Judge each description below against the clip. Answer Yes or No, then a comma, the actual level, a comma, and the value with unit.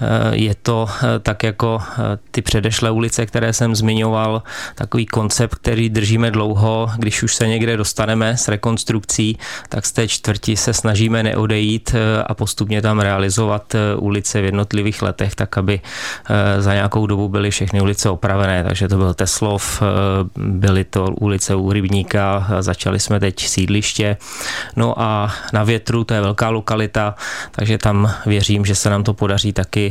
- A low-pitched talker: Yes, low, 105 Hz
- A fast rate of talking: No, average, 155 wpm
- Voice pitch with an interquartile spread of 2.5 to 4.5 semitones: No, narrow, 1.9 semitones